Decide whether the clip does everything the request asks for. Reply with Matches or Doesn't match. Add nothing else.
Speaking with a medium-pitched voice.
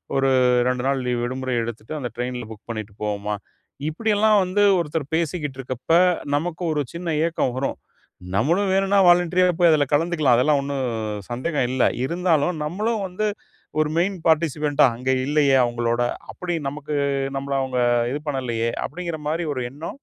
Matches